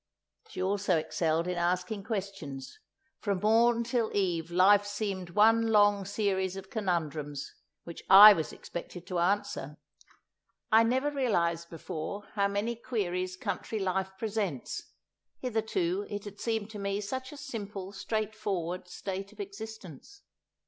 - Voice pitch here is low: No, high, 200 Hz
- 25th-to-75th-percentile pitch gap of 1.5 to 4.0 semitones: Yes, average, 3.3 semitones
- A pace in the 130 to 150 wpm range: Yes, slow, 135 wpm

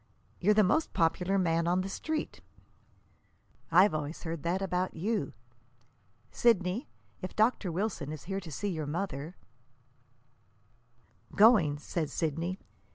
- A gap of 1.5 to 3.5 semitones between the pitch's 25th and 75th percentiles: No, average, 4.2 semitones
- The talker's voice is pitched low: No, medium, 175 Hz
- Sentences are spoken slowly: Yes, slow, 130 wpm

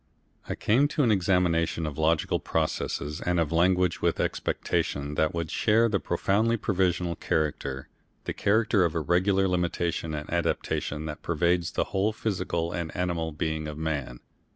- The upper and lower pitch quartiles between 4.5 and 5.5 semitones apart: No, average, 3.2 semitones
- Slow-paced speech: No, average, 160 wpm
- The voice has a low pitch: Yes, very low, 85 Hz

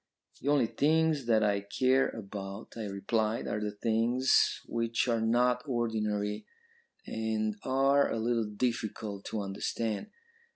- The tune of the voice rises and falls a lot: No, average, 2.7 semitones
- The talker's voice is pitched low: Yes, low, 115 Hz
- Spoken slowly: Yes, slow, 130 wpm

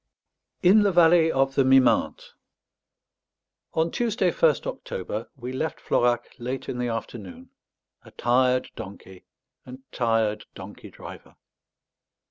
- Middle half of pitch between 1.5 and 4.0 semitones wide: No, average, 5.2 semitones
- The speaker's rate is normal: No, slow, 115 wpm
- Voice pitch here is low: Yes, low, 130 Hz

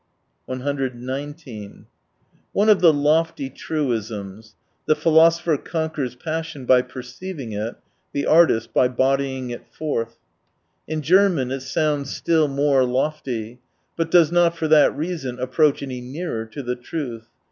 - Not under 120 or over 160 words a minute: Yes, slow, 135 wpm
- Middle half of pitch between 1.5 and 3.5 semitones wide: No, average, 4.2 semitones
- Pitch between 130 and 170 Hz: Yes, medium, 140 Hz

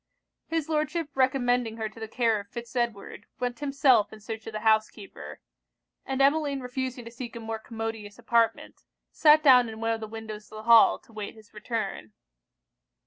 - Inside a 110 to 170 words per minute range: No, average, 185 wpm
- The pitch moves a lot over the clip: No, average, 3.0 semitones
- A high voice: Yes, high, 230 Hz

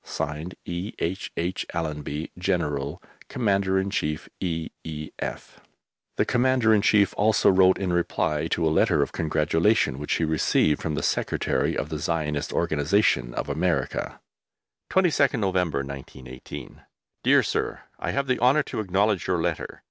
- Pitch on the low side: Yes, very low, 85 Hz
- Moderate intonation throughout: Yes, average, 4.7 semitones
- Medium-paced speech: Yes, average, 145 wpm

